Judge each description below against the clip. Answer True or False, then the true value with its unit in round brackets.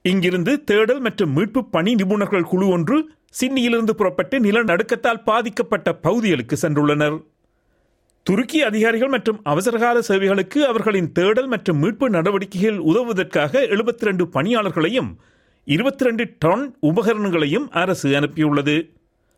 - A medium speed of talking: True (100 wpm)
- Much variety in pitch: True (5.9 semitones)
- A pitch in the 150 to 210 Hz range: True (200 Hz)